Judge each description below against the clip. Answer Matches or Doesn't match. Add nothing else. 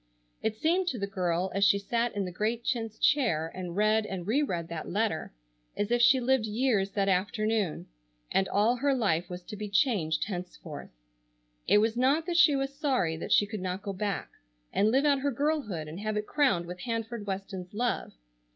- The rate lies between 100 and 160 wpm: Doesn't match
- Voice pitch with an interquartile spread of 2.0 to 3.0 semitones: Doesn't match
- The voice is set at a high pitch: Matches